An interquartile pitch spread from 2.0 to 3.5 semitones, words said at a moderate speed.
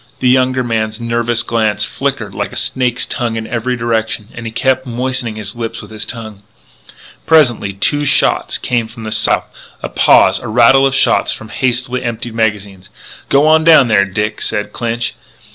Yes: narrow, 2.6 semitones; average, 175 wpm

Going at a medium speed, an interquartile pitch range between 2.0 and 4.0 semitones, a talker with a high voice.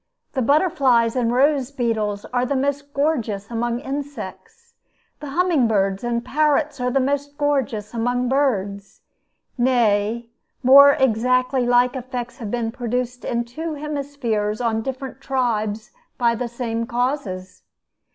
No: slow, 130 wpm; average, 3.4 semitones; very high, 250 Hz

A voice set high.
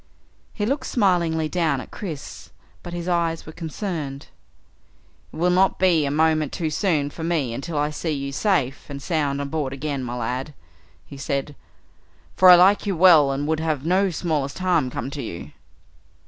No: medium, 155 Hz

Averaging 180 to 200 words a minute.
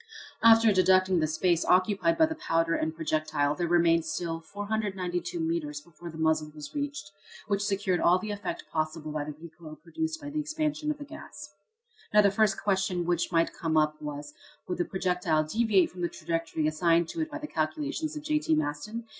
Yes: average, 190 wpm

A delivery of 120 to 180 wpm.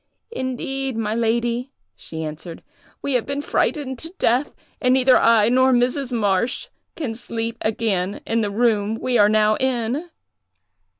Yes: average, 145 wpm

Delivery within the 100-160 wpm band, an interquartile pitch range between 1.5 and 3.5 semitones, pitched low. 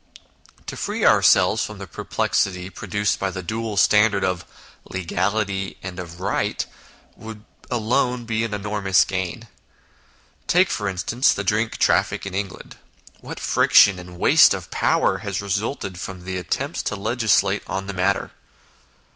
Yes: average, 145 wpm; average, 2.8 semitones; low, 100 Hz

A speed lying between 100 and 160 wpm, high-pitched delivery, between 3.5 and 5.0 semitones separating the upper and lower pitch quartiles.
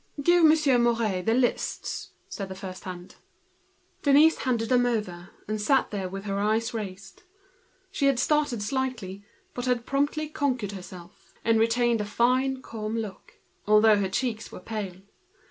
Yes: average, 145 wpm; high, 225 Hz; average, 4.6 semitones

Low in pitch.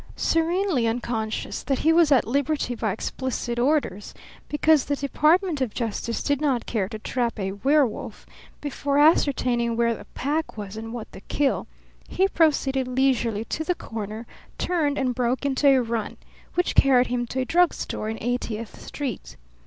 No: very high, 255 Hz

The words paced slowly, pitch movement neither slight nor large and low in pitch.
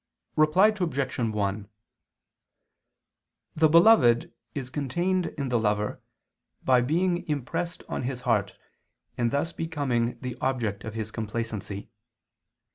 No: slow, 115 wpm; wide, 6.1 semitones; low, 125 Hz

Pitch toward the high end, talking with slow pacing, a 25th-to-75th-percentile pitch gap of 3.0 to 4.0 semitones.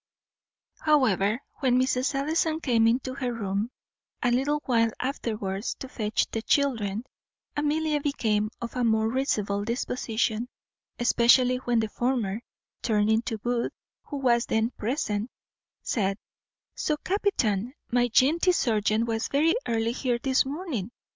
Yes: high, 240 Hz; slow, 130 wpm; average, 3.5 semitones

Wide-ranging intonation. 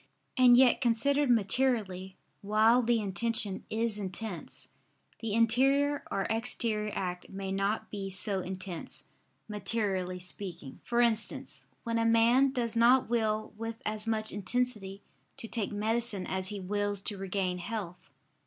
No: average, 3.3 semitones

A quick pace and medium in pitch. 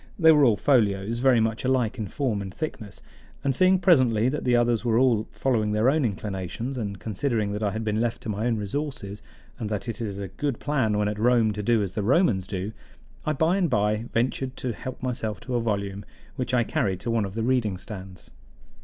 No: fast, 225 wpm; low, 115 Hz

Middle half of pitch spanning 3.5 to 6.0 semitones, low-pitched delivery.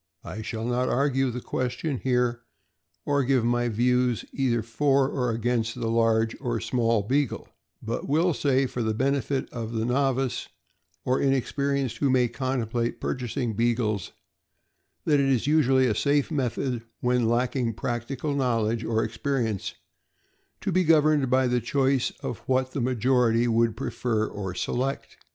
No: average, 2.7 semitones; low, 125 Hz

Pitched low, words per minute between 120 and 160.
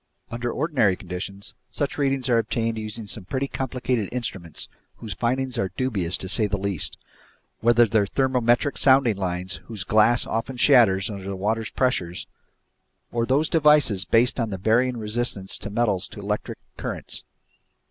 Yes: low, 115 Hz; average, 155 wpm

